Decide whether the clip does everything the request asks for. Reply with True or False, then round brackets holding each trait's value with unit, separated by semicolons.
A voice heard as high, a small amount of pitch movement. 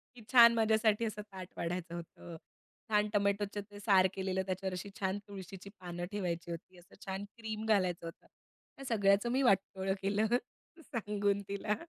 True (200 Hz; 2.3 semitones)